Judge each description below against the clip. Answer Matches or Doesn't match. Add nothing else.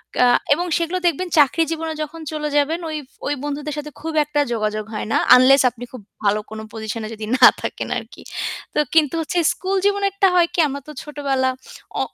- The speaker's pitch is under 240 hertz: Doesn't match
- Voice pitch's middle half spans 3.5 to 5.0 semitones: Matches